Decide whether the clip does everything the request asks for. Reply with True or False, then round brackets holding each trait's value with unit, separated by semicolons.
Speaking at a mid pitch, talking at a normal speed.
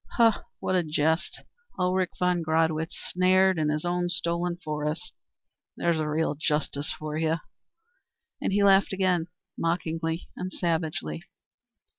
False (165 Hz; 120 wpm)